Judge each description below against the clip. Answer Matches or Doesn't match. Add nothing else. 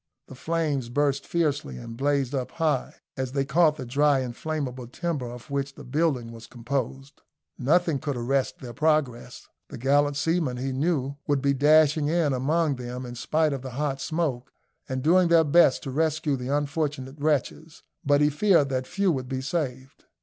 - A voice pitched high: Doesn't match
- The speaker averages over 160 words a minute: Matches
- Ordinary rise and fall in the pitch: Matches